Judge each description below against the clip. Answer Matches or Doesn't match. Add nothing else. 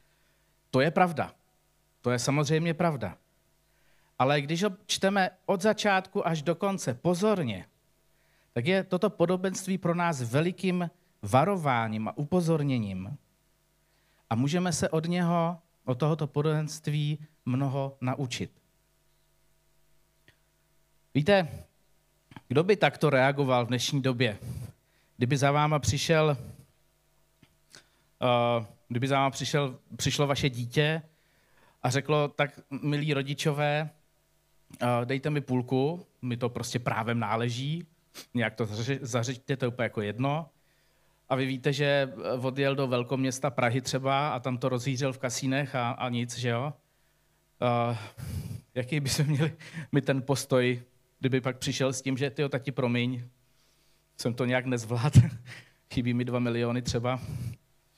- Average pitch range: Matches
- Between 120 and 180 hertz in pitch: Matches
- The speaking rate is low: Doesn't match